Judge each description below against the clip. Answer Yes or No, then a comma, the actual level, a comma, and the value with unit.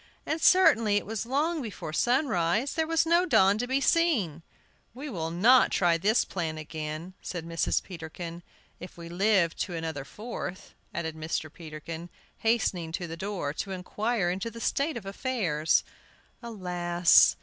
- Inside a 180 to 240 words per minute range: No, average, 155 wpm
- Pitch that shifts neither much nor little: No, wide, 6.1 semitones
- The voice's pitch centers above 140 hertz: Yes, medium, 185 Hz